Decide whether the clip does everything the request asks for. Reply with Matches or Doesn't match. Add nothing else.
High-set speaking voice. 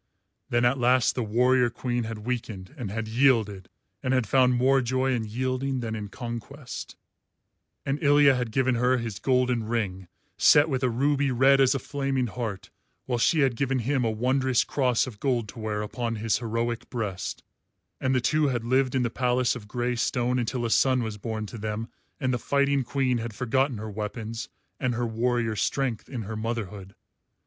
Doesn't match